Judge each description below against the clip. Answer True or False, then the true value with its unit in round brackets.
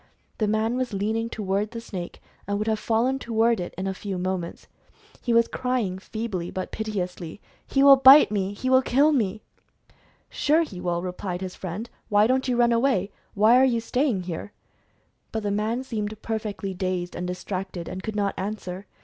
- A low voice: False (210 Hz)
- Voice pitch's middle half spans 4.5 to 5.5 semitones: False (3.8 semitones)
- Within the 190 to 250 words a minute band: True (195 wpm)